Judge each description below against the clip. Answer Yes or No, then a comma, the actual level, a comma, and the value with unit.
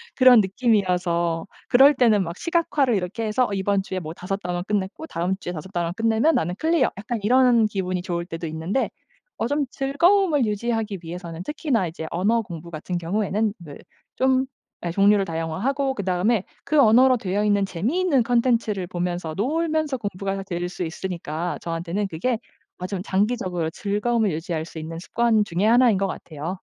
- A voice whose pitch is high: Yes, high, 200 Hz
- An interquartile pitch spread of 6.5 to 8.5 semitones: No, wide, 5.4 semitones